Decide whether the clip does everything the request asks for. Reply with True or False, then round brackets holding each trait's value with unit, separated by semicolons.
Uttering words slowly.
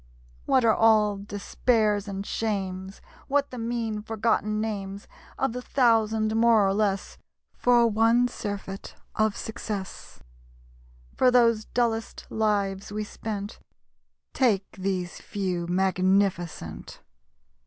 True (110 wpm)